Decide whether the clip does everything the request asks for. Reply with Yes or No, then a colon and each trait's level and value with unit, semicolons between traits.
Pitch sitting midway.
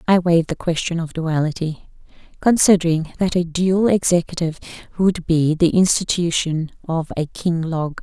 Yes: medium, 170 Hz